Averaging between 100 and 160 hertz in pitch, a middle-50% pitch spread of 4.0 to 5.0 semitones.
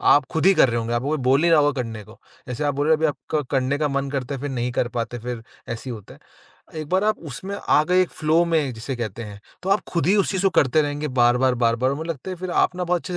Yes: medium, 140 Hz; average, 4.7 semitones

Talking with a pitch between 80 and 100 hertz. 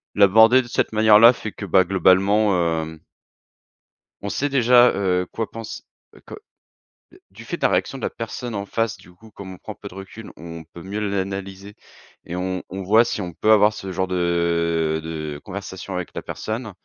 Yes: very low, 95 Hz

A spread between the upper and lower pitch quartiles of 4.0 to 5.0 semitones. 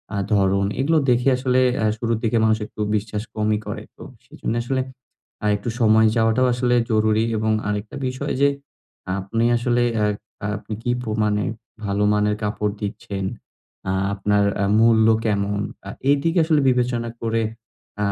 No: average, 2.7 semitones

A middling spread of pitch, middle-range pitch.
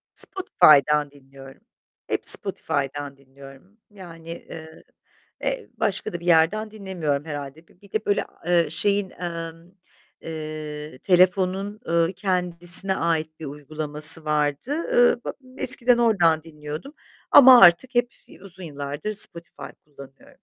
Yes: average, 4.7 semitones; medium, 165 Hz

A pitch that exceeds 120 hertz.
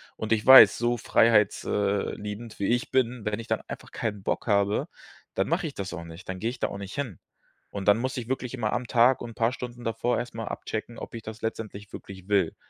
No: low, 115 Hz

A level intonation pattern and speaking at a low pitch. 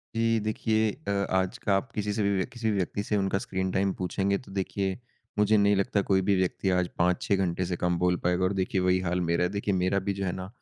Yes: narrow, 1.7 semitones; very low, 95 Hz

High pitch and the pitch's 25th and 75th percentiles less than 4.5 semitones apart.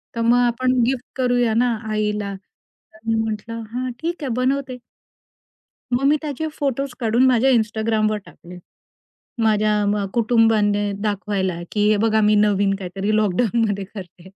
Yes: high, 220 Hz; average, 3.0 semitones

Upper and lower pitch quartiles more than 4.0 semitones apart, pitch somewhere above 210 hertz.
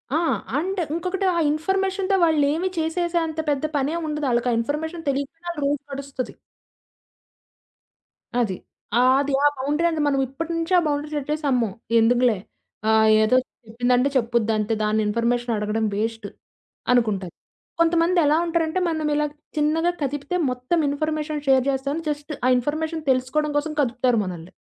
Yes: average, 4.5 semitones; very high, 285 Hz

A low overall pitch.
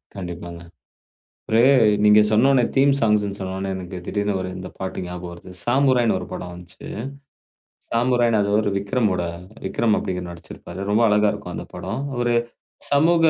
Yes: low, 105 Hz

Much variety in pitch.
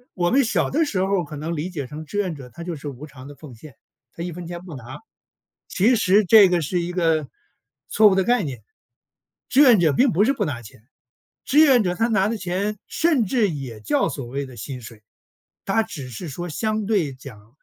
Yes: wide, 7.0 semitones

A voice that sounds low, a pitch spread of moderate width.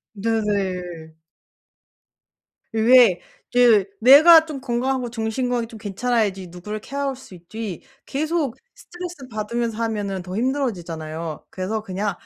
No: high, 225 Hz; average, 4.9 semitones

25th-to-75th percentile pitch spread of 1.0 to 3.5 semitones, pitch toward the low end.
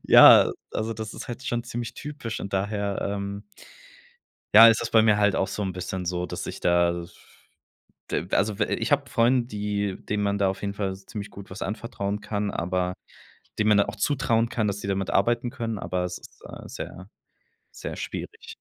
Yes: average, 2.8 semitones; low, 105 Hz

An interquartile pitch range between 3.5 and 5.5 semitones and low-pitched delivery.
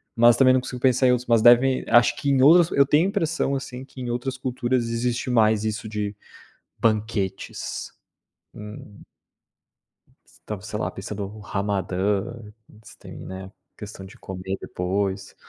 Yes: average, 4.1 semitones; low, 115 Hz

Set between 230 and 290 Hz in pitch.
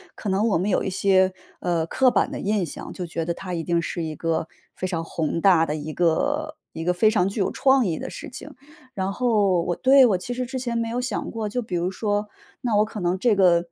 No: high, 195 Hz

